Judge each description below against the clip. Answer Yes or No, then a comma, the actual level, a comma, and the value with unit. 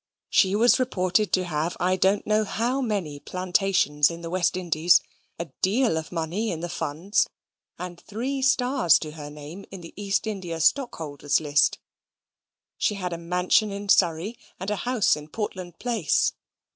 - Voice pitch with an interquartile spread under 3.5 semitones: No, average, 4.1 semitones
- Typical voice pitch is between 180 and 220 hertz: Yes, medium, 185 Hz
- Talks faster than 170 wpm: No, average, 165 wpm